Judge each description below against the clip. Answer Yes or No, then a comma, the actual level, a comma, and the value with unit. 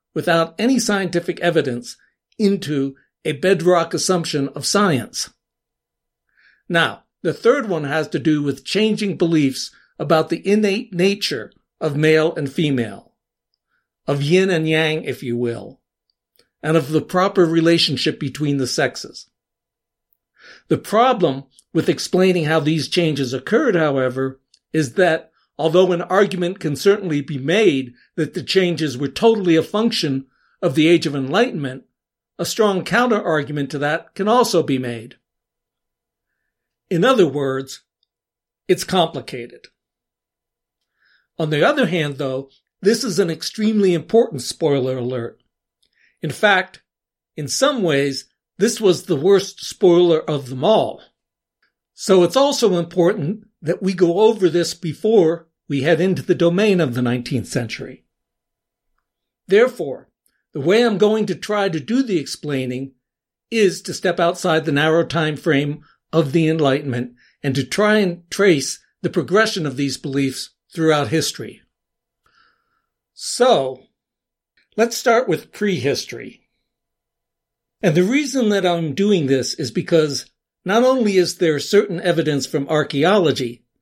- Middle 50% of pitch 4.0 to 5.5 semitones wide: Yes, average, 5.2 semitones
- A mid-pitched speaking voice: Yes, medium, 165 Hz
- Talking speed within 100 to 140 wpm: Yes, slow, 135 wpm